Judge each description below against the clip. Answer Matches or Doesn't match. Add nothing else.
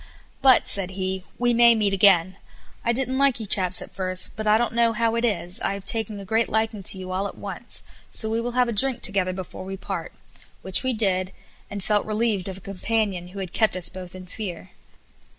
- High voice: Matches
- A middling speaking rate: Doesn't match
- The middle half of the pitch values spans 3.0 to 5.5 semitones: Matches